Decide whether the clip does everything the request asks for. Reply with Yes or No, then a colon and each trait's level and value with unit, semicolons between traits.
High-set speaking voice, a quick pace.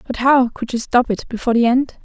Yes: high, 245 Hz; fast, 265 wpm